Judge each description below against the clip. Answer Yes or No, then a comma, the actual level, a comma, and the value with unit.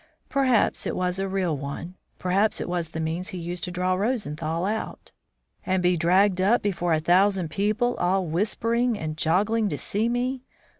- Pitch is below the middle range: No, medium, 185 Hz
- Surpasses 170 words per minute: Yes, average, 180 wpm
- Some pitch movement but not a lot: Yes, average, 3.5 semitones